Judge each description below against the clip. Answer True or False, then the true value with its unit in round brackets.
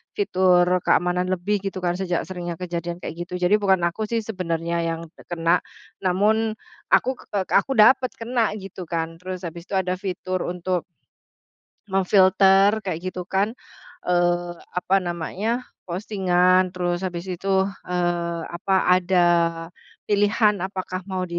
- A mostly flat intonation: True (1.9 semitones)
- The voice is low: False (185 Hz)